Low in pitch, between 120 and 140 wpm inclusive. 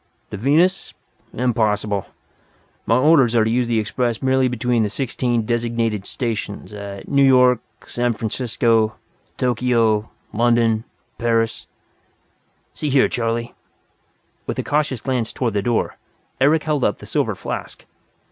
Yes: low, 120 Hz; slow, 135 wpm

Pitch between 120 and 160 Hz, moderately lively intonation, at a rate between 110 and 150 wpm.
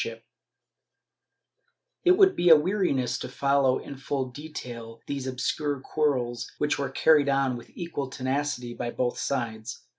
Yes: low, 135 Hz; average, 3.2 semitones; average, 145 wpm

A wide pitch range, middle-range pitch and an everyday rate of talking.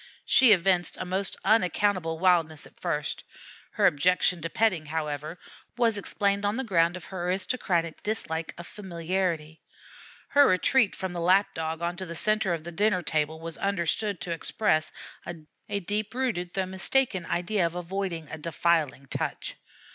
No: average, 3.3 semitones; medium, 180 Hz; average, 155 wpm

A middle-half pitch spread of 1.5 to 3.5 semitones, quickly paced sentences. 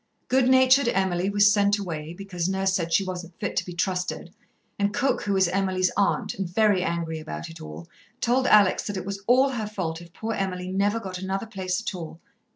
Yes: narrow, 2.6 semitones; fast, 210 wpm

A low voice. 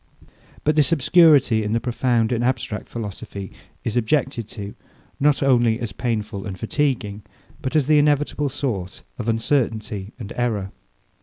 Yes: low, 120 Hz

